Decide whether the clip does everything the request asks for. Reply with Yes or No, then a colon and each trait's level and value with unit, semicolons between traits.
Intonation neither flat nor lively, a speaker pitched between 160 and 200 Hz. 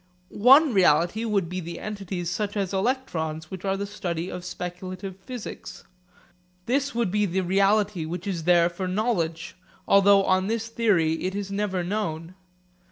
Yes: average, 3.1 semitones; high, 190 Hz